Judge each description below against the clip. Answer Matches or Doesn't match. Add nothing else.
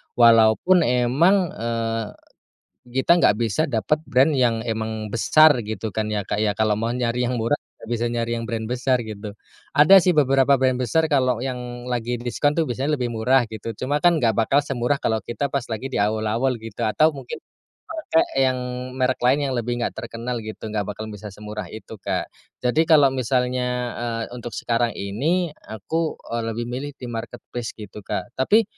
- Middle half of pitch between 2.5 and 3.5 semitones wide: Matches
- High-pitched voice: Doesn't match